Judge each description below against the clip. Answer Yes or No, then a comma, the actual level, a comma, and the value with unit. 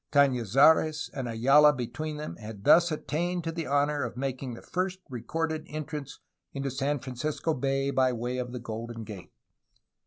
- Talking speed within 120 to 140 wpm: No, average, 165 wpm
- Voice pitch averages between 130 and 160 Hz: Yes, low, 135 Hz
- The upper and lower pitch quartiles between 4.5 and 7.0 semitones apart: No, average, 3.9 semitones